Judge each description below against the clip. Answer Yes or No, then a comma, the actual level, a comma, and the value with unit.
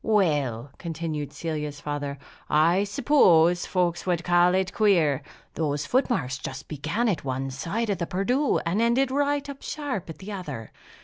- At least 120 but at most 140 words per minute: No, average, 165 wpm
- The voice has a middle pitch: Yes, medium, 175 Hz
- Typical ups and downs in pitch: No, wide, 6.4 semitones